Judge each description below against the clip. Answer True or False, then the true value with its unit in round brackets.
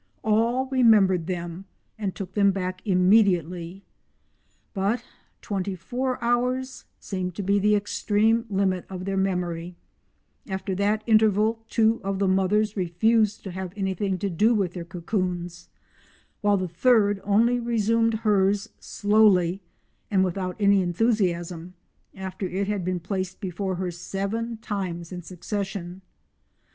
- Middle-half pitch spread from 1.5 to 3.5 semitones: True (2.8 semitones)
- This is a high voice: True (195 Hz)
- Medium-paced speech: False (130 wpm)